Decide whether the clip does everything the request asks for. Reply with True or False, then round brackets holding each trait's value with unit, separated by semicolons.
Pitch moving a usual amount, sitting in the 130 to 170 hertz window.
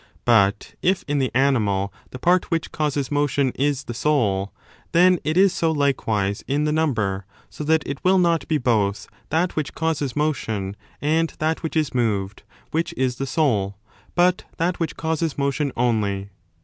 False (6.2 semitones; 140 Hz)